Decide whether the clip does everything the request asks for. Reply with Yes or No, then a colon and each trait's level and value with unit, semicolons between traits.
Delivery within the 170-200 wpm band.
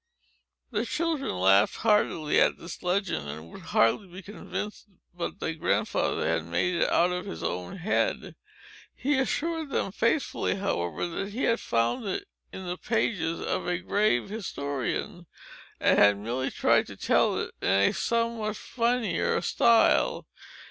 No: average, 150 wpm